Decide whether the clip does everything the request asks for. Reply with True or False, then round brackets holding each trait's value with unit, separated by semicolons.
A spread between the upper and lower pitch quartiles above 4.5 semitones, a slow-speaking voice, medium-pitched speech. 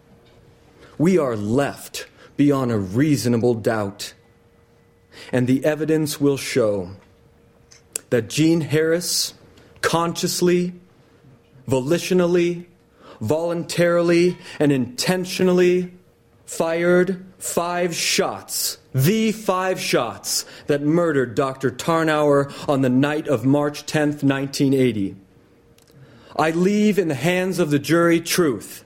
True (5.6 semitones; 95 wpm; 150 Hz)